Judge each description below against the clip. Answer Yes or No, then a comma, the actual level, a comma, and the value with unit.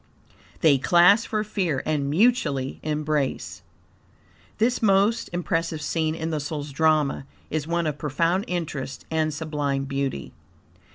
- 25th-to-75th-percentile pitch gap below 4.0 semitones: Yes, average, 3.2 semitones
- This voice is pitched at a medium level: Yes, medium, 155 Hz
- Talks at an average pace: No, slow, 125 wpm